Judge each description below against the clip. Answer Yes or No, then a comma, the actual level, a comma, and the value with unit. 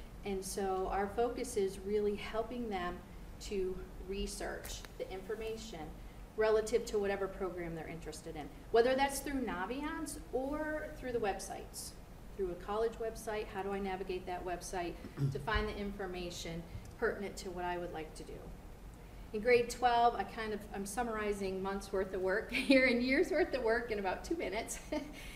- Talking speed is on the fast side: No, average, 170 wpm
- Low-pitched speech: No, high, 205 Hz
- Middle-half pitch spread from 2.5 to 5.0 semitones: Yes, average, 4.2 semitones